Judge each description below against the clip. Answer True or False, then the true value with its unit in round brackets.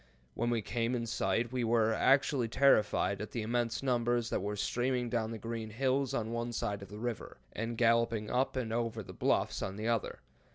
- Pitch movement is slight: True (1.6 semitones)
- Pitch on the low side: True (115 Hz)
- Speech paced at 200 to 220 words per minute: True (205 wpm)